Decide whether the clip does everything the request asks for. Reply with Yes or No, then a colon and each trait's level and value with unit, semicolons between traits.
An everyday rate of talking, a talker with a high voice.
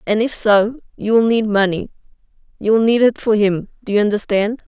Yes: average, 175 wpm; high, 215 Hz